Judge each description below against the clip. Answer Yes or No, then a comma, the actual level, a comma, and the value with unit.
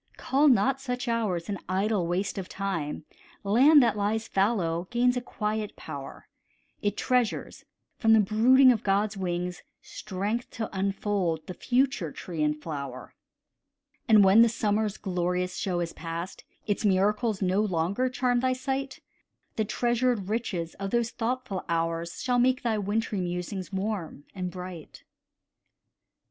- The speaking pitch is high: Yes, high, 205 Hz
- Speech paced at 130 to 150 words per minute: Yes, average, 145 wpm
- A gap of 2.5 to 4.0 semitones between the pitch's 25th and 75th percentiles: No, average, 4.7 semitones